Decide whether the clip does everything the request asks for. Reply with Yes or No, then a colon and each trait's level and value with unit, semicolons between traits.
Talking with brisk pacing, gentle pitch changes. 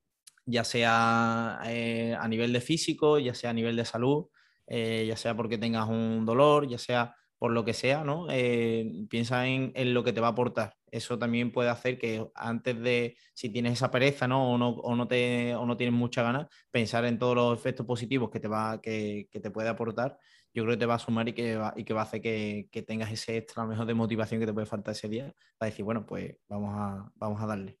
Yes: fast, 235 wpm; narrow, 1.5 semitones